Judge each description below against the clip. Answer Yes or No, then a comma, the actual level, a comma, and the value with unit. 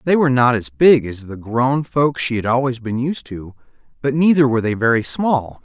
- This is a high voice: No, low, 125 Hz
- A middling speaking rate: No, fast, 225 wpm